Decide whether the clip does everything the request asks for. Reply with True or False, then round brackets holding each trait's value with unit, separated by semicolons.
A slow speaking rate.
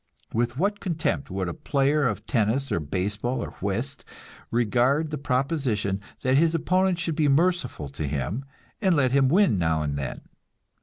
False (165 wpm)